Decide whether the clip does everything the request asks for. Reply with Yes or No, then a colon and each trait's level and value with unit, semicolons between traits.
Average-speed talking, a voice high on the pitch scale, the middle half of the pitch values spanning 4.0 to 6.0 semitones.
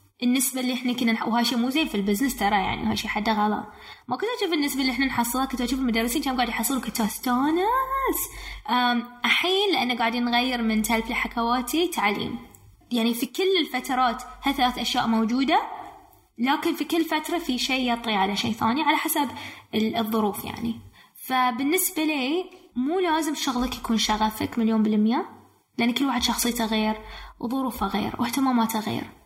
No: fast, 160 wpm; very high, 250 Hz; average, 4.3 semitones